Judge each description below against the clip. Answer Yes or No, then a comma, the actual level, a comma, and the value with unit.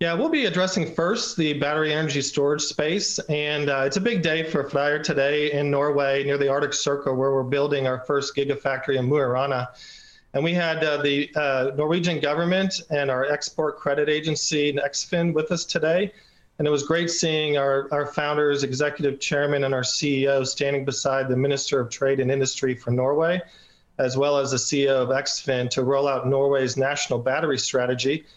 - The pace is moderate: Yes, average, 185 wpm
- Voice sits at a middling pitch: Yes, medium, 145 Hz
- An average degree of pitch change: No, narrow, 2.1 semitones